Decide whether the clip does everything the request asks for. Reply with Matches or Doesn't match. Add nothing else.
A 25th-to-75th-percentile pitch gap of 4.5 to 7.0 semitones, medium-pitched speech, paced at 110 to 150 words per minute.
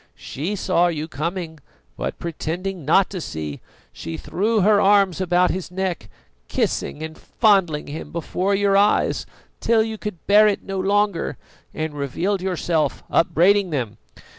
Doesn't match